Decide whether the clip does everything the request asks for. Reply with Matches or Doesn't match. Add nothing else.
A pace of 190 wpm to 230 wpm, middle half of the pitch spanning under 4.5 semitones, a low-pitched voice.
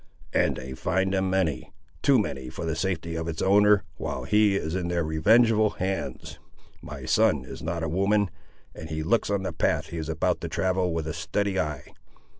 Matches